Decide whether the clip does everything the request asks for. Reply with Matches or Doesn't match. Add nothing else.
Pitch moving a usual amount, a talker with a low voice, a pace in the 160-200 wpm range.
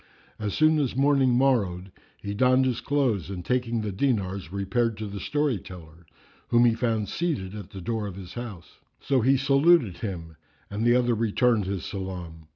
Matches